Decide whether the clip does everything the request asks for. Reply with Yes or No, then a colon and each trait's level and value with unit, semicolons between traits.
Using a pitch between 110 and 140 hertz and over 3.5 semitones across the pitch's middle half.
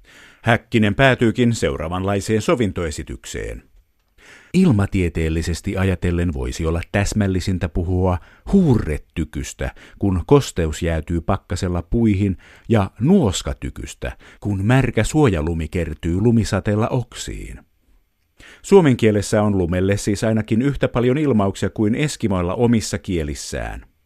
No: low, 100 Hz; average, 5.2 semitones